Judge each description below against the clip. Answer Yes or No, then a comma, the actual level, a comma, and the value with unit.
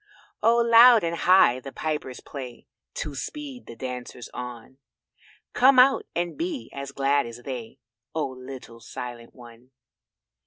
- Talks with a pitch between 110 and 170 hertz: Yes, low, 135 Hz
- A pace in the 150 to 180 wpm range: No, average, 140 wpm